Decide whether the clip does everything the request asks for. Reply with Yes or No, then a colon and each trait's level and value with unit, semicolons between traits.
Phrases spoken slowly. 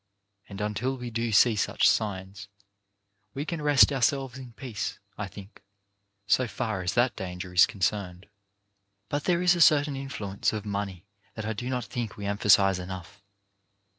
No: average, 165 wpm